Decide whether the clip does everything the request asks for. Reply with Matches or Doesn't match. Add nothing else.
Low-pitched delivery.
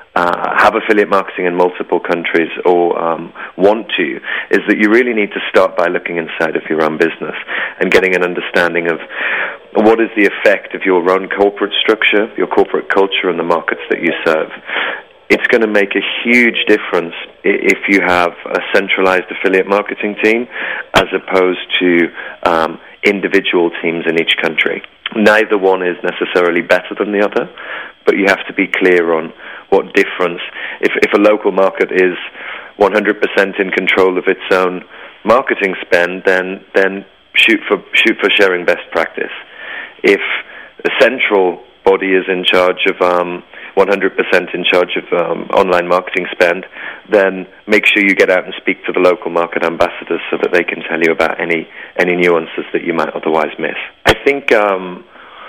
Matches